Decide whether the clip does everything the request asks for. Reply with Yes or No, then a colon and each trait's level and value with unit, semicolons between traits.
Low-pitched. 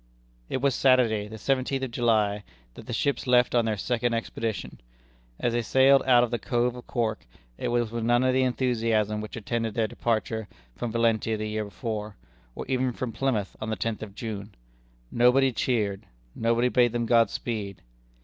Yes: low, 115 Hz